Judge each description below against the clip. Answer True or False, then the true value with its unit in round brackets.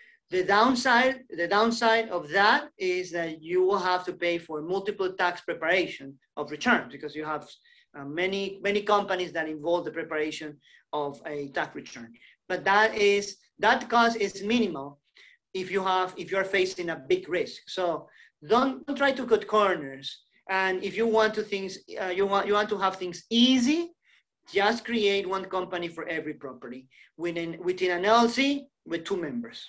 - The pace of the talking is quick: False (170 wpm)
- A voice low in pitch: False (195 Hz)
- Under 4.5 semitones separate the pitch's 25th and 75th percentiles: False (4.8 semitones)